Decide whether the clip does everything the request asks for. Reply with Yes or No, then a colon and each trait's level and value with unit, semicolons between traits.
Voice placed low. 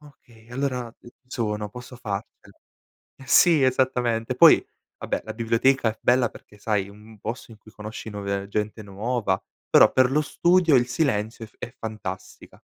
Yes: low, 115 Hz